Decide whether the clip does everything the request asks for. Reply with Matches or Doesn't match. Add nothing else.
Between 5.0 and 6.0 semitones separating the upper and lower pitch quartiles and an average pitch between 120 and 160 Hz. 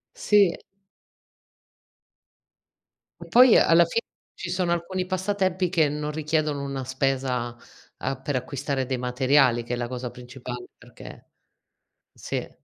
Matches